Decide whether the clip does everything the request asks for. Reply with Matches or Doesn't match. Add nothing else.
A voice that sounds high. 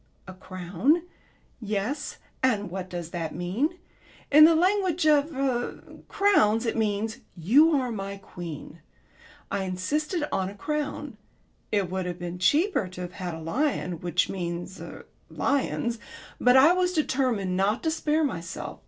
Matches